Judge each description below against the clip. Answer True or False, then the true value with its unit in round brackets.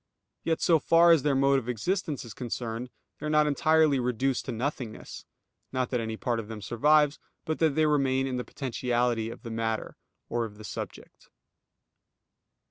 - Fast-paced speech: False (180 wpm)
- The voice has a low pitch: True (130 Hz)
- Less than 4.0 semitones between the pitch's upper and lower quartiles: False (4.5 semitones)